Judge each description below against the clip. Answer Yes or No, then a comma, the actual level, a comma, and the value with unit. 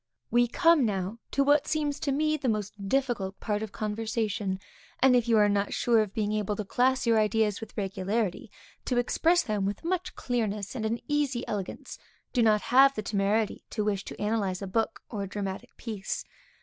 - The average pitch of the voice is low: No, high, 220 Hz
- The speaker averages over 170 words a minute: Yes, average, 195 wpm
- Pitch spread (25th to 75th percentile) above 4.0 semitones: No, average, 3.4 semitones